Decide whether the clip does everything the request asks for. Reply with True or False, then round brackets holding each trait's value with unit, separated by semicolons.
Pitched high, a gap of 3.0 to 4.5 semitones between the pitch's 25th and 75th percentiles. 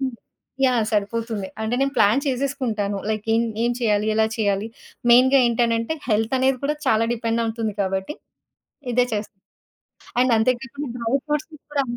True (230 Hz; 3.3 semitones)